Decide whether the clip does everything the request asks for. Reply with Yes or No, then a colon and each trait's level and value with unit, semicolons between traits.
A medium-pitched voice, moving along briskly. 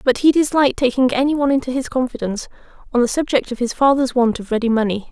No: very high, 255 Hz; fast, 225 wpm